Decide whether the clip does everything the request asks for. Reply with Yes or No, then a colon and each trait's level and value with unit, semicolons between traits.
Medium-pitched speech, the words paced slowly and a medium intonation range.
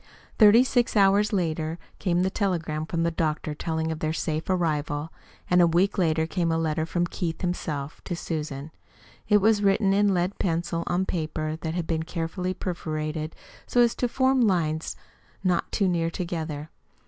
No: medium, 170 Hz; average, 170 wpm; average, 3.1 semitones